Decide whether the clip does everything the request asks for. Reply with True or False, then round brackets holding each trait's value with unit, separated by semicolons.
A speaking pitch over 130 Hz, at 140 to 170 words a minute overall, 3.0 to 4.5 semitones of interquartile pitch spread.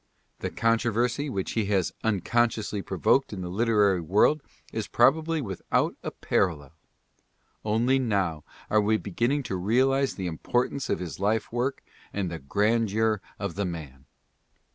False (105 Hz; 155 wpm; 4.2 semitones)